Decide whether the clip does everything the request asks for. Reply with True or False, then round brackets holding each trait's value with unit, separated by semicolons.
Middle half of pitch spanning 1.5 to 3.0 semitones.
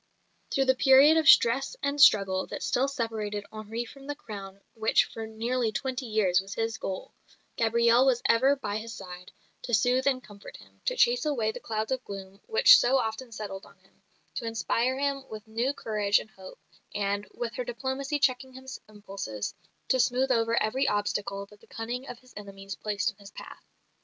False (4.2 semitones)